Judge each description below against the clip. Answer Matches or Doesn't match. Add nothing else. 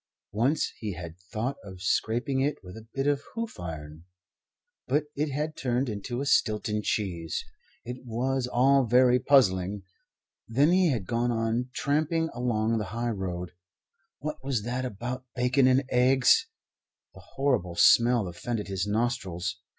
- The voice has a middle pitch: Doesn't match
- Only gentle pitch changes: Doesn't match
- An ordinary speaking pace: Matches